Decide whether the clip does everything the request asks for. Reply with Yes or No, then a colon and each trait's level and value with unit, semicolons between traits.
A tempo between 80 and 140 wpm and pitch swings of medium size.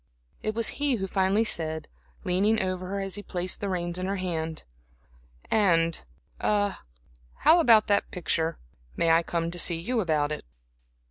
No: average, 165 wpm; average, 3.5 semitones